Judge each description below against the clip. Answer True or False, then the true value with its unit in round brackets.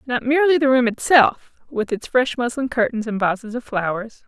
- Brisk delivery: False (195 wpm)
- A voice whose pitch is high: True (240 Hz)